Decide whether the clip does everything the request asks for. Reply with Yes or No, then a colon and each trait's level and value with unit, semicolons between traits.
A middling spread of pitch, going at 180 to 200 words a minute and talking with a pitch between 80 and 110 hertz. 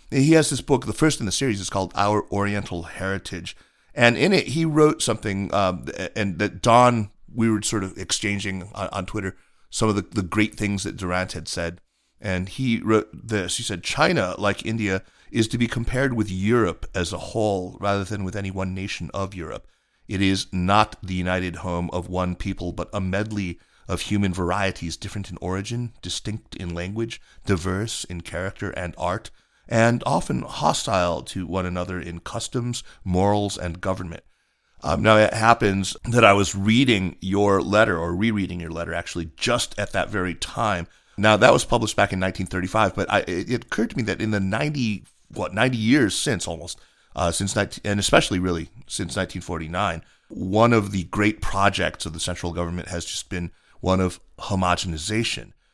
Yes: average, 3.2 semitones; average, 185 wpm; low, 100 Hz